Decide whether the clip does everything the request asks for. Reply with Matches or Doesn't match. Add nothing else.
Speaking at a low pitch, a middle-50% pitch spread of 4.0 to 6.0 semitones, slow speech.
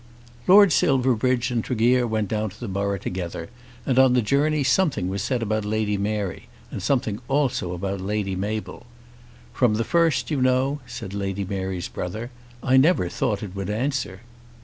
Doesn't match